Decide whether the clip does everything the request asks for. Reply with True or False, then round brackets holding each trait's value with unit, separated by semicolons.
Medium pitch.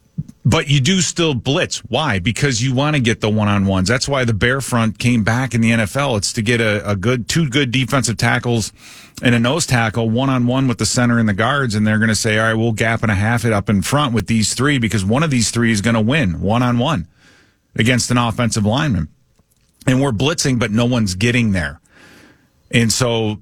False (120 Hz)